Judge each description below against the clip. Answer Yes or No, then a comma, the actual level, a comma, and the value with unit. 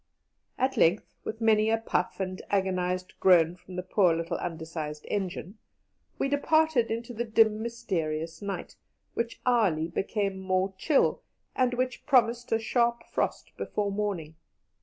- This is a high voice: Yes, high, 200 Hz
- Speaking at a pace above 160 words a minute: No, average, 140 wpm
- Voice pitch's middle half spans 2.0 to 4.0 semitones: No, average, 4.4 semitones